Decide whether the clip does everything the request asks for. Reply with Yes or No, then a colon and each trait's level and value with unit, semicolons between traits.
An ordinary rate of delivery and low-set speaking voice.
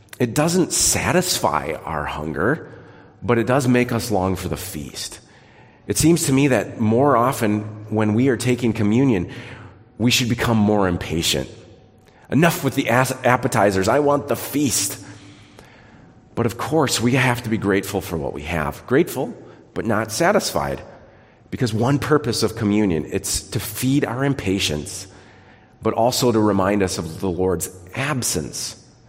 Yes: average, 155 wpm; low, 110 Hz